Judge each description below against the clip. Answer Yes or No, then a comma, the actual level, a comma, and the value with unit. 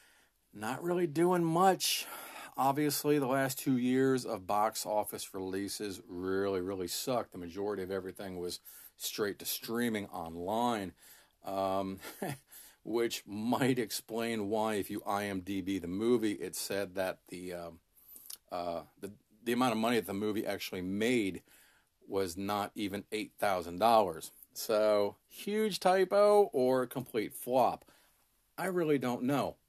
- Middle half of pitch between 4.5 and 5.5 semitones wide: Yes, average, 5.1 semitones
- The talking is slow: Yes, slow, 130 wpm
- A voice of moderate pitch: No, low, 105 Hz